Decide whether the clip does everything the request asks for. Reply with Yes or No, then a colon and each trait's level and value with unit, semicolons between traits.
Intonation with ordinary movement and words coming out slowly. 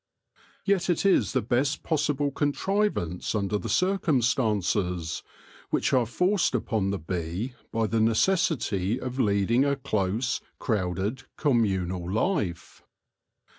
No: wide, 6.7 semitones; slow, 120 wpm